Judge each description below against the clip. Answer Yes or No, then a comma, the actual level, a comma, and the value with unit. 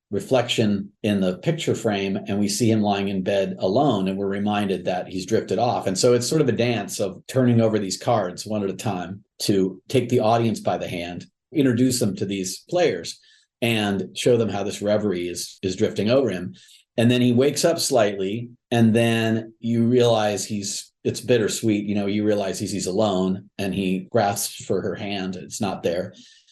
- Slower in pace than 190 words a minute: No, average, 200 wpm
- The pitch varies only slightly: No, average, 3.1 semitones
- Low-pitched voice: Yes, low, 105 Hz